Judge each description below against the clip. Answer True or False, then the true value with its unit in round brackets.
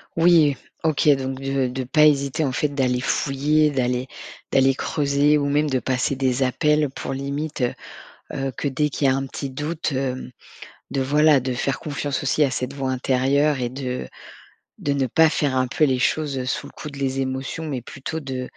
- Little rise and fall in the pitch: True (2.1 semitones)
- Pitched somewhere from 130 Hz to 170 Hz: True (135 Hz)